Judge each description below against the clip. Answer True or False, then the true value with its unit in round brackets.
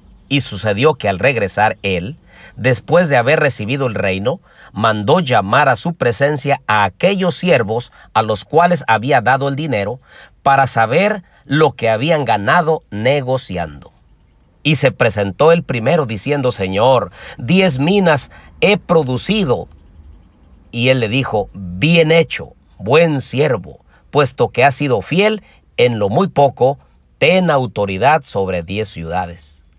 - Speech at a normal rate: True (135 wpm)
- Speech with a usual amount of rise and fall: False (7.5 semitones)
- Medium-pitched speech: False (130 Hz)